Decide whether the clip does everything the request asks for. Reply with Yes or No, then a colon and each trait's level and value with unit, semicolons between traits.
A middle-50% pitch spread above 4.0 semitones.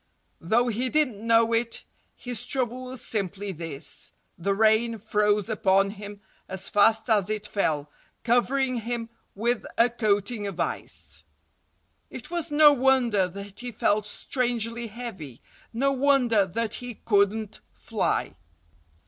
No: average, 3.3 semitones